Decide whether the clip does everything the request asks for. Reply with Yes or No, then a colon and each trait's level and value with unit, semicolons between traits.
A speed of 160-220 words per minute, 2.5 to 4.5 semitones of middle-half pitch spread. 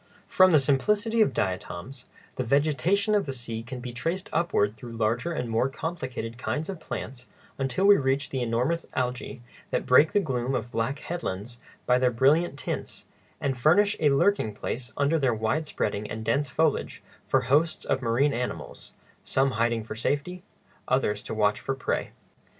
No: average, 170 wpm; average, 5.1 semitones